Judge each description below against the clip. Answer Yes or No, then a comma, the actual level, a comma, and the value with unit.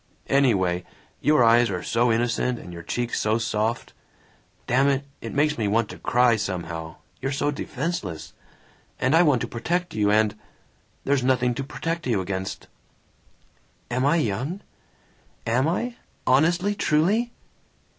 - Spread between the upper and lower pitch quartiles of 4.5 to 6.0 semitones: Yes, wide, 5.5 semitones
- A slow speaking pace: No, average, 145 wpm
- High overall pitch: No, low, 125 Hz